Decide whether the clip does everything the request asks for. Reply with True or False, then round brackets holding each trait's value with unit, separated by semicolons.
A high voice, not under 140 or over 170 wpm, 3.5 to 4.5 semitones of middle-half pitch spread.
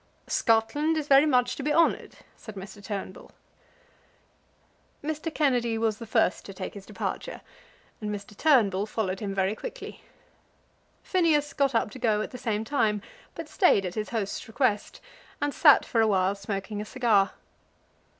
False (225 Hz; 160 wpm; 5.3 semitones)